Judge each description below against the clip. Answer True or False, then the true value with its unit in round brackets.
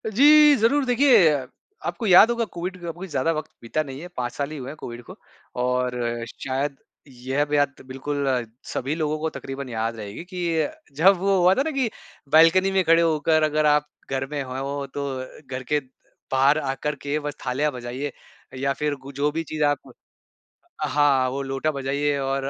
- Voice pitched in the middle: True (145 Hz)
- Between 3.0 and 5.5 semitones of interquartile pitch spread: True (3.7 semitones)